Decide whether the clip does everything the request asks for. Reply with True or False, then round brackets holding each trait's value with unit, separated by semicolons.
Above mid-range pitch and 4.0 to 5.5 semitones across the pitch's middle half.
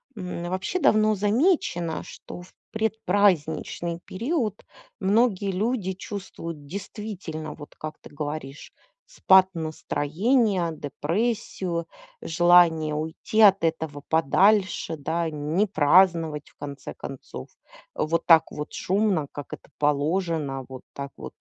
False (175 Hz; 4.5 semitones)